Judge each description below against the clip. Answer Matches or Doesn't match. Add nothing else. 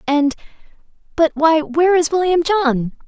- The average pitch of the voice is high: Matches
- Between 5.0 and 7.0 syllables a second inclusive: Doesn't match